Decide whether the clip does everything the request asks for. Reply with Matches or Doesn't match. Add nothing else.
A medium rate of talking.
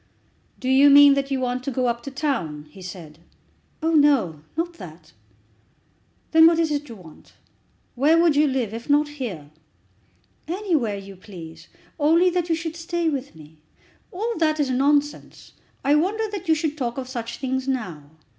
Matches